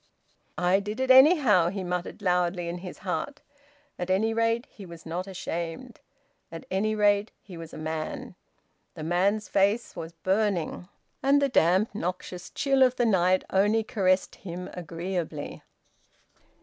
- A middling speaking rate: Yes, average, 150 wpm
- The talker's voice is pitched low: No, medium, 185 Hz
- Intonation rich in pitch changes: No, average, 3.7 semitones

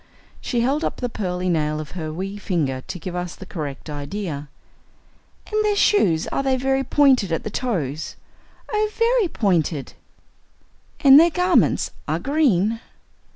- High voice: Yes, high, 195 Hz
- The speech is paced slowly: No, average, 150 wpm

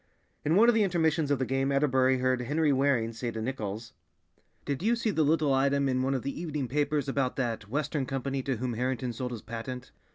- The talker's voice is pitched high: No, low, 135 Hz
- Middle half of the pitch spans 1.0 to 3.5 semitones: Yes, average, 2.8 semitones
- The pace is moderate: No, fast, 220 wpm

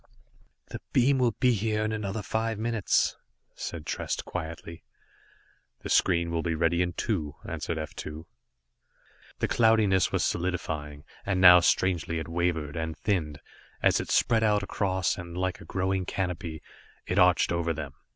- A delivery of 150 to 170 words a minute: Yes, average, 155 wpm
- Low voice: Yes, very low, 90 Hz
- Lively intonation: No, average, 3.7 semitones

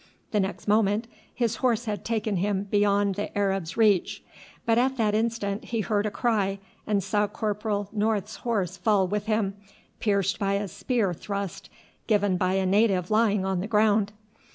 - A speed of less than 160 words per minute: No, average, 170 wpm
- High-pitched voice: Yes, high, 205 Hz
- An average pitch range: No, narrow, 1.9 semitones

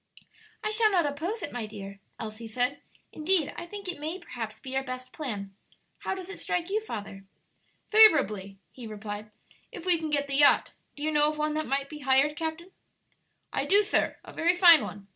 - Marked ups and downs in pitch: Yes, wide, 6.9 semitones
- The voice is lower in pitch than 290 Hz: No, very high, 295 Hz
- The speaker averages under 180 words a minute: No, average, 200 wpm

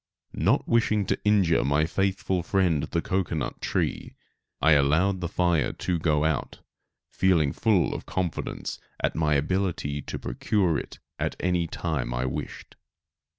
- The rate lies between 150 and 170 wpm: No, slow, 135 wpm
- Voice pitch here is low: Yes, very low, 85 Hz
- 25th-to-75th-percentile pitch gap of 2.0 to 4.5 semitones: Yes, average, 3.9 semitones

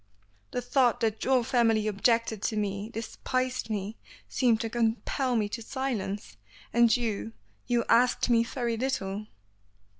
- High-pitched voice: Yes, high, 230 Hz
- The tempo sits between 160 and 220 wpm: No, average, 140 wpm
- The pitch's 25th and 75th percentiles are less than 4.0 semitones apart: Yes, narrow, 2.5 semitones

